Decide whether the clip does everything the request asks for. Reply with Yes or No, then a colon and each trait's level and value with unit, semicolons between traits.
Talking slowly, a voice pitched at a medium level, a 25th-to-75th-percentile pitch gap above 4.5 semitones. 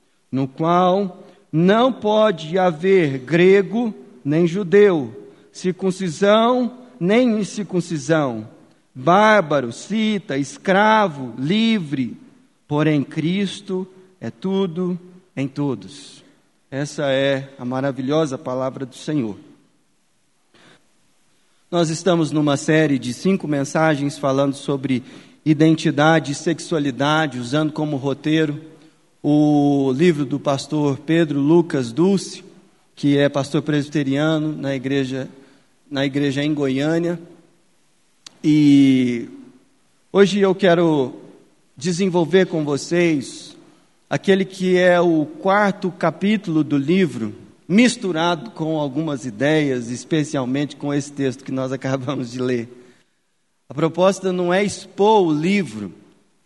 Yes: slow, 100 wpm; medium, 155 Hz; average, 4.9 semitones